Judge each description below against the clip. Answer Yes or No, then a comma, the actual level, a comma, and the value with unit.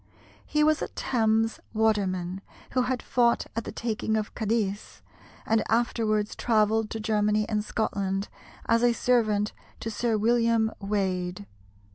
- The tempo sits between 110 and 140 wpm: Yes, slow, 135 wpm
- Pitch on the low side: No, high, 220 Hz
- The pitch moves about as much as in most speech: No, narrow, 1.8 semitones